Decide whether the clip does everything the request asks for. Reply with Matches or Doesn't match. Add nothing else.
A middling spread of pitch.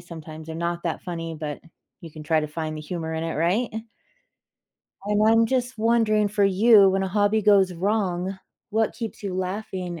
Matches